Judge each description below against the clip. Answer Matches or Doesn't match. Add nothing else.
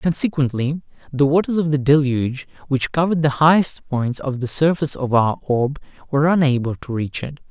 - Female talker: Doesn't match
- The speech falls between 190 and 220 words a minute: Doesn't match